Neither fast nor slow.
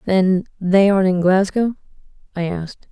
No: slow, 125 wpm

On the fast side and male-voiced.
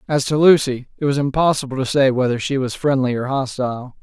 Yes: fast, 210 wpm; male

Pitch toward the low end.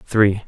Yes: low, 100 Hz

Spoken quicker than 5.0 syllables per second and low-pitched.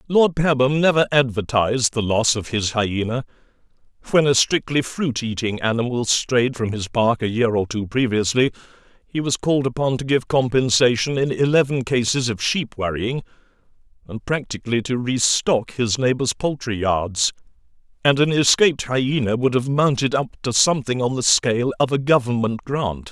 No: 4.9 syllables/s; low, 125 Hz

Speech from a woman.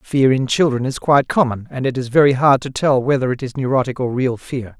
No: male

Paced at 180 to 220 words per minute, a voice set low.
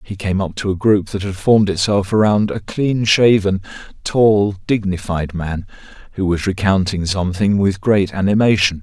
No: average, 165 wpm; low, 100 Hz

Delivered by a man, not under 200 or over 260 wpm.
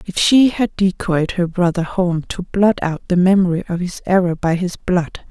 No: female; fast, 205 wpm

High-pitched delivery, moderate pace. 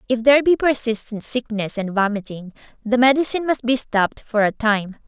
Yes: high, 235 Hz; average, 175 wpm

